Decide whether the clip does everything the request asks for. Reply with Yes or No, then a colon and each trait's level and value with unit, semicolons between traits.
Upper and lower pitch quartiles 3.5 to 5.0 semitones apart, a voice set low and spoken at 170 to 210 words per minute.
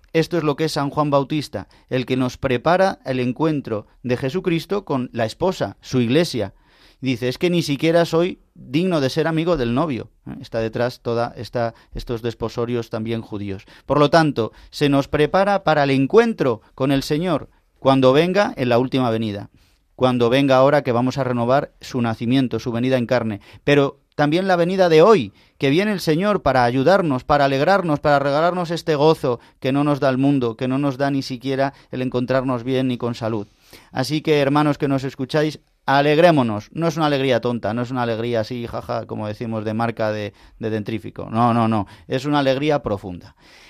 Yes: average, 4.1 semitones; low, 130 Hz; fast, 190 wpm